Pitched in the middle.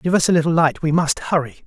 Yes: medium, 160 Hz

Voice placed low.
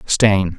Yes: very low, 95 Hz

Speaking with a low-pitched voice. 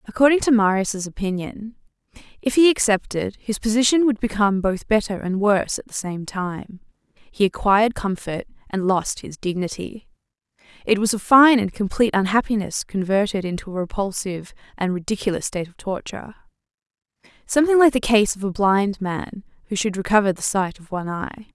No: high, 205 Hz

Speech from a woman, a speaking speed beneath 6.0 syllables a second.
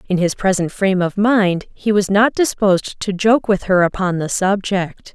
Yes: female; 4.7 syllables/s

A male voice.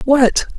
No: female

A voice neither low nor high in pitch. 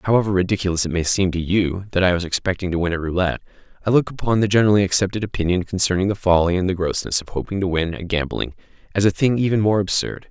No: very low, 95 Hz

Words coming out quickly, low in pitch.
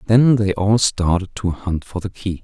Yes: fast, 220 wpm; low, 100 Hz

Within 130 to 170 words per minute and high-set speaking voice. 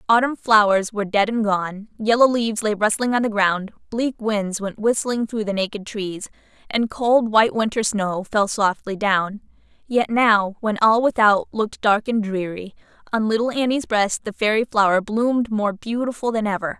No: average, 180 wpm; high, 215 Hz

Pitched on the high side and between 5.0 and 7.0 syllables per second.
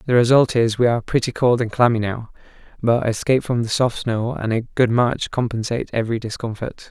No: low, 120 Hz; 5.8 syllables/s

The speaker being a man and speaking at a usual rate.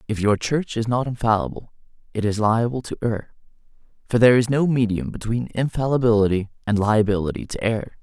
Yes: male; average, 165 wpm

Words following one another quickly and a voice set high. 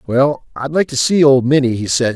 No: fast, 280 wpm; low, 135 Hz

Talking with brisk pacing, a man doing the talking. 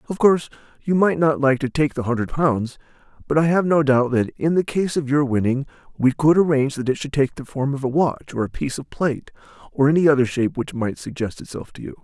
Yes: fast, 245 wpm; male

